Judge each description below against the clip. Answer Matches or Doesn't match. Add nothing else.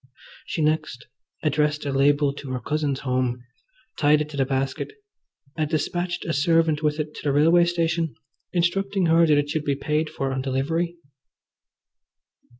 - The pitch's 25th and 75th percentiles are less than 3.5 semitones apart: Matches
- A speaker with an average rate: Matches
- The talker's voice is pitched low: Doesn't match